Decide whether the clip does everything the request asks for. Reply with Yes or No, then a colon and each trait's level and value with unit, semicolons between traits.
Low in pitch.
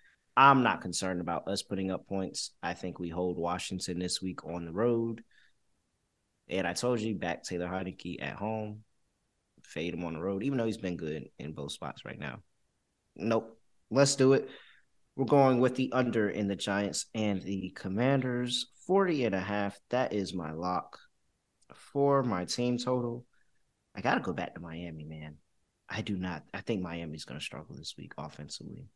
Yes: very low, 95 Hz